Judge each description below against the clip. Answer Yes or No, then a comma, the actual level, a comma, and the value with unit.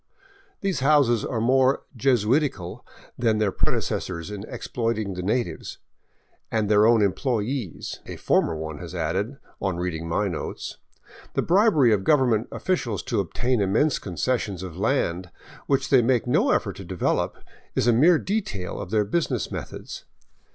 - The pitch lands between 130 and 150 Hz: No, low, 110 Hz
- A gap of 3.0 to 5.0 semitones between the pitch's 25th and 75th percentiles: No, wide, 5.4 semitones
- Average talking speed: Yes, average, 160 wpm